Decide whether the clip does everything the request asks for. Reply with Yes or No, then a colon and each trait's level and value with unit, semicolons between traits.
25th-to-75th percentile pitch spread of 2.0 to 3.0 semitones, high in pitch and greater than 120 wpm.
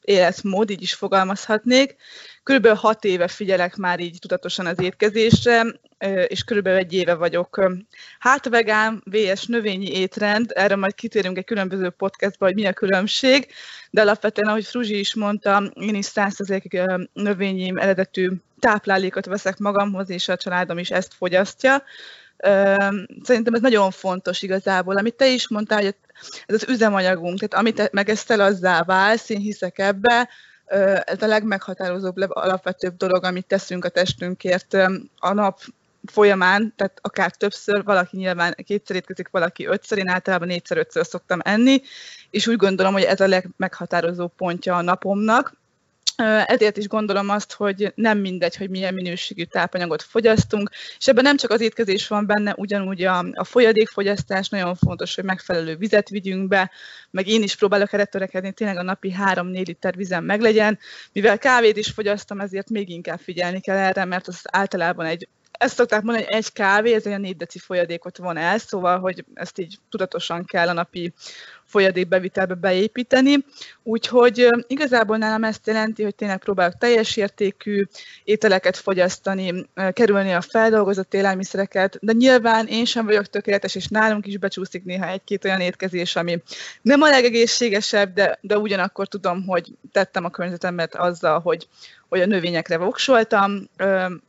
Yes: average, 2.7 semitones; high, 195 Hz; fast, 155 wpm